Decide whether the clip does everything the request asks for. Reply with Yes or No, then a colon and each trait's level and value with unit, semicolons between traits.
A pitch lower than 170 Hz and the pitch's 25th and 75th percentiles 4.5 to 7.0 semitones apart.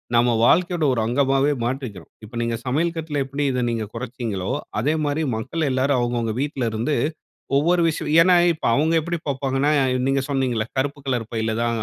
No: low, 135 Hz; average, 4.0 semitones